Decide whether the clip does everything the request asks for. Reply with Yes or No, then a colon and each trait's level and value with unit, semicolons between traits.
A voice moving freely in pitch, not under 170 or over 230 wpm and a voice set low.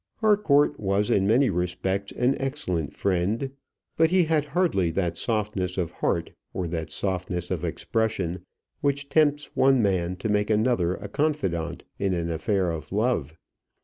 No: wide, 7.3 semitones; average, 150 wpm; low, 100 Hz